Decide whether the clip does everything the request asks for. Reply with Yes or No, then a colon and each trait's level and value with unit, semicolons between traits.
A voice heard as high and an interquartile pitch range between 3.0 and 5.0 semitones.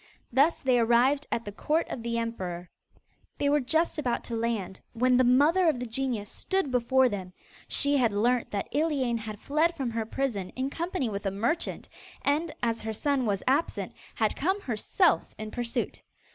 Yes: very high, 250 Hz; average, 4.3 semitones